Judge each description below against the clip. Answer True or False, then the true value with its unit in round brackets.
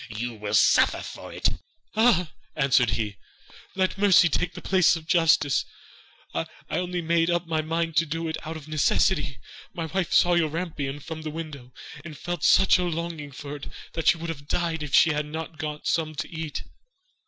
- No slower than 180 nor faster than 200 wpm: True (190 wpm)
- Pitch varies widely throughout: False (2.6 semitones)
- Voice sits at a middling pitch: True (160 Hz)